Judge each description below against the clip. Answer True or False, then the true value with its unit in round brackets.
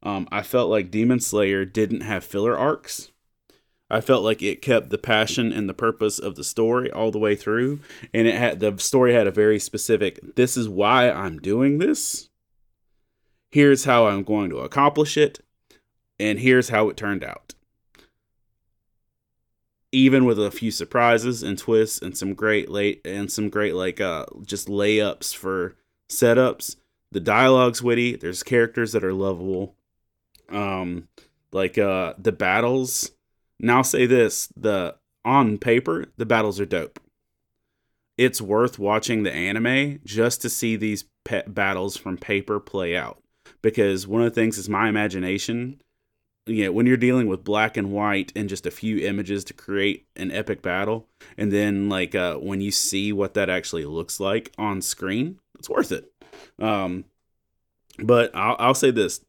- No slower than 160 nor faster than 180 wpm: True (165 wpm)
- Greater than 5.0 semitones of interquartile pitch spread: False (2.8 semitones)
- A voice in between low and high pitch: False (110 Hz)